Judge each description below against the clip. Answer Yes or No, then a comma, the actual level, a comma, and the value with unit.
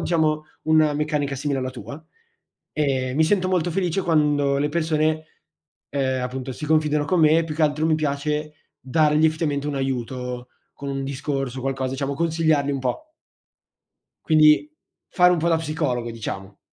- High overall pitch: No, medium, 150 Hz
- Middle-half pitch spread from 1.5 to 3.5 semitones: Yes, average, 2.7 semitones